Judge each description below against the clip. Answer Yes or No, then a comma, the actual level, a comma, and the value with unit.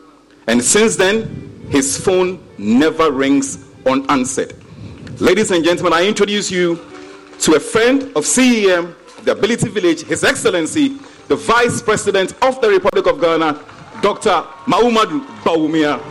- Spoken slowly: Yes, slow, 130 wpm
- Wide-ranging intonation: Yes, wide, 7.5 semitones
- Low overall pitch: No, medium, 185 Hz